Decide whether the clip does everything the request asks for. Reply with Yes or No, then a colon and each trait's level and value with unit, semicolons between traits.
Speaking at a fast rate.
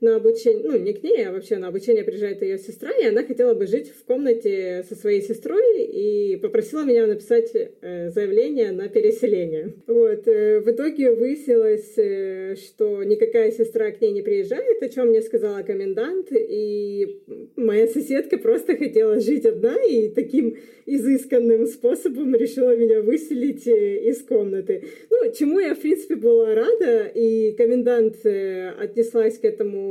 No: average, 150 wpm